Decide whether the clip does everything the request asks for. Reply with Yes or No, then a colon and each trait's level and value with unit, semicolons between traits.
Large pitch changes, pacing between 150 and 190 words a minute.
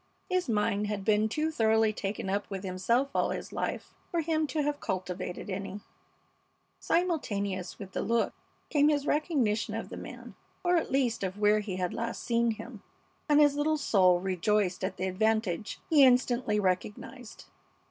Yes: wide, 6.3 semitones; average, 170 wpm